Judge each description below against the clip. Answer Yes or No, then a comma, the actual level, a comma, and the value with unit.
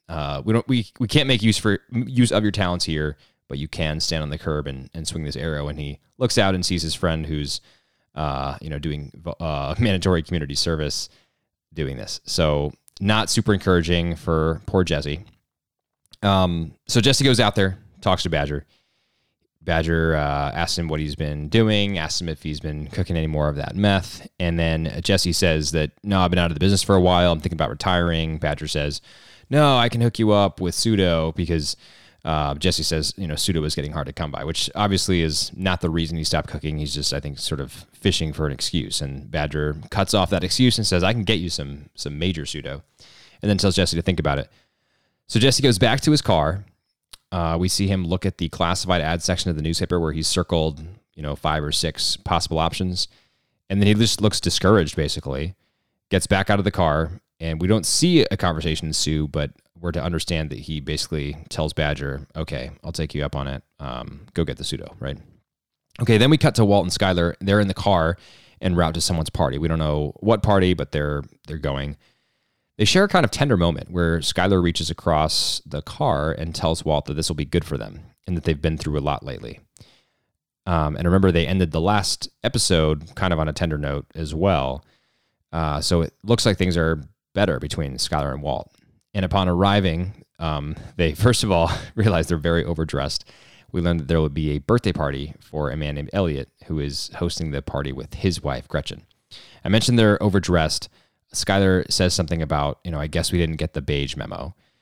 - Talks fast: Yes, fast, 215 wpm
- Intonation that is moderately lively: Yes, average, 4.1 semitones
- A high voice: No, very low, 85 Hz